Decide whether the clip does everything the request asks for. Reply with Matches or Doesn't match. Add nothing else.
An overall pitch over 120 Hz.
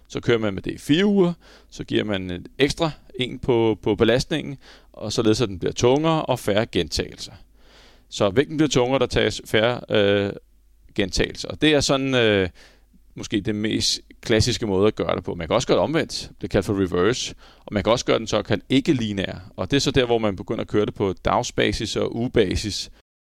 Doesn't match